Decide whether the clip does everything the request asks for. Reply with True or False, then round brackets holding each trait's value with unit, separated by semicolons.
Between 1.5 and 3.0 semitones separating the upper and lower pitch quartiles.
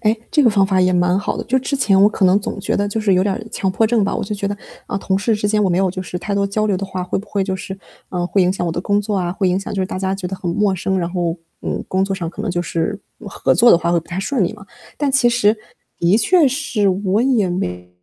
True (2.4 semitones)